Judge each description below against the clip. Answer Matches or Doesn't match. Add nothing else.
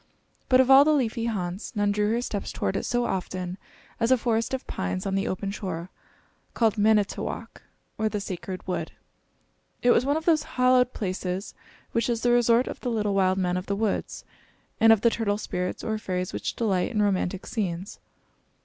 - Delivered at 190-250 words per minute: Matches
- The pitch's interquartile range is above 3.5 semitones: Matches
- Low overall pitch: Doesn't match